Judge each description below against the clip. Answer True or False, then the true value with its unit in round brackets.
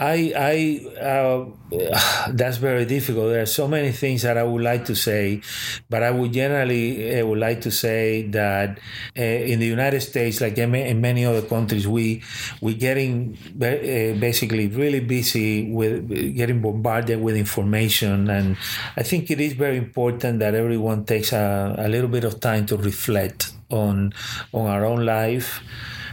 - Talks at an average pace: True (160 wpm)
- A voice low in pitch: True (115 Hz)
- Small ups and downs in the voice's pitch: True (2.3 semitones)